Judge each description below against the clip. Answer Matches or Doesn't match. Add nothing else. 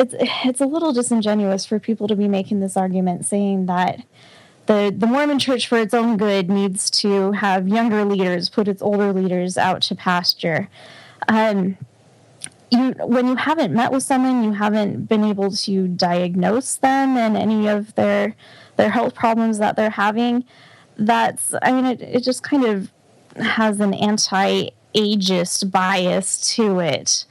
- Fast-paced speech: Doesn't match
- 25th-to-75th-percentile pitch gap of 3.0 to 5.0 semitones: Matches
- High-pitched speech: Matches